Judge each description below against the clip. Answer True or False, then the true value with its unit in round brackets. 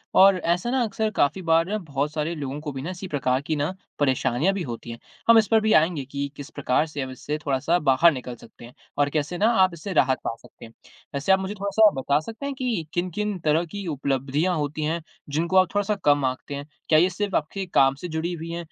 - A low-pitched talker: False (155 Hz)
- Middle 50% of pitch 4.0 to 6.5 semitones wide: True (4.9 semitones)